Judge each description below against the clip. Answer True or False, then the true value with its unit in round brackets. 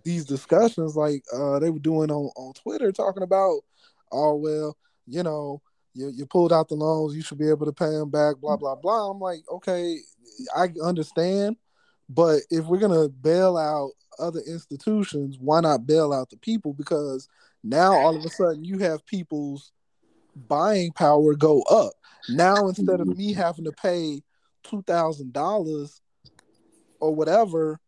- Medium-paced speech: True (165 wpm)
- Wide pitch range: False (3.2 semitones)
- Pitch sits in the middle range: True (160 Hz)